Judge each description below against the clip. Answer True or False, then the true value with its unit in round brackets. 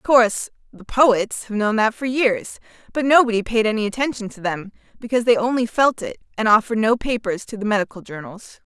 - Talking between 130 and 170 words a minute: False (200 wpm)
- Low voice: False (225 Hz)